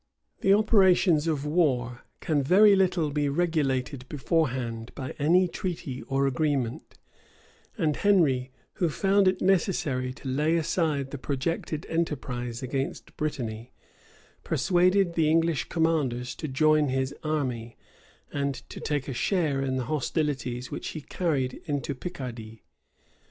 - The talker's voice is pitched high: No, medium, 145 Hz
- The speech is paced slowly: Yes, slow, 130 wpm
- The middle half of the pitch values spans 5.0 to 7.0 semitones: No, average, 4.3 semitones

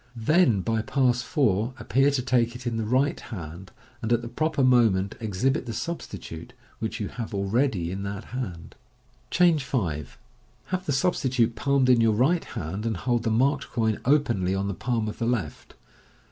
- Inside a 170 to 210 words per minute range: Yes, average, 180 wpm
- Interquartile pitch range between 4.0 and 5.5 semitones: Yes, average, 4.4 semitones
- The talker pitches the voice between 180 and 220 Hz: No, low, 115 Hz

